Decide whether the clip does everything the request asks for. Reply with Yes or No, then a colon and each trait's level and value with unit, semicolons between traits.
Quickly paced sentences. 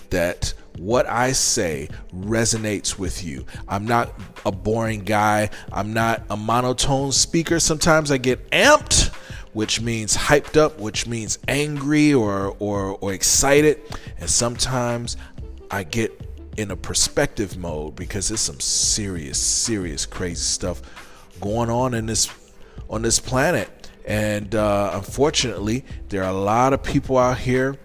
No: average, 140 wpm